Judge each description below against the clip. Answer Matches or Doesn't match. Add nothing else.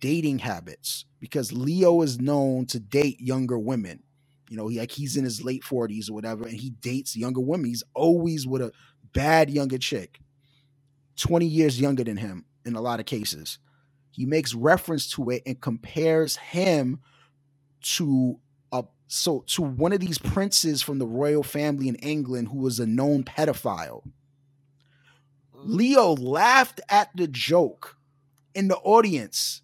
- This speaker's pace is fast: Doesn't match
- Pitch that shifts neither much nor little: Matches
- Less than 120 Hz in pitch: Doesn't match